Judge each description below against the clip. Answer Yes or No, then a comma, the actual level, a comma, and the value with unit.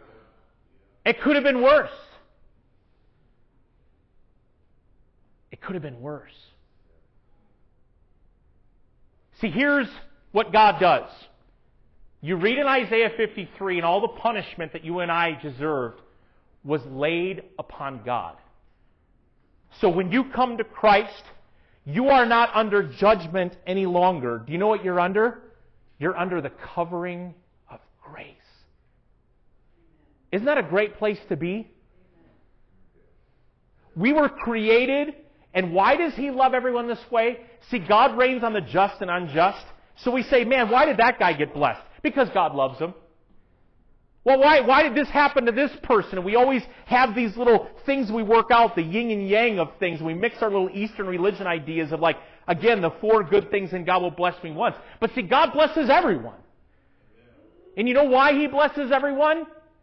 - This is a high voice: Yes, high, 210 Hz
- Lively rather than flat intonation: Yes, wide, 6.5 semitones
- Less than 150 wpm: No, average, 155 wpm